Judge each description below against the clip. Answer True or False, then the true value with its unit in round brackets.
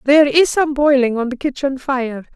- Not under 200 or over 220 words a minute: True (205 wpm)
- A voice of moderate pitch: False (270 Hz)